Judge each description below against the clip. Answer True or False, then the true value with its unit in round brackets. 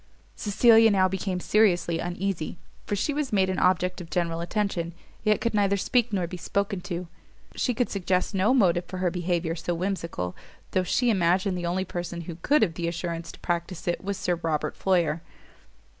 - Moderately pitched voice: True (180 Hz)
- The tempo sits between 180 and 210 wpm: True (185 wpm)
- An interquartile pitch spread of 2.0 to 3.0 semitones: True (2.6 semitones)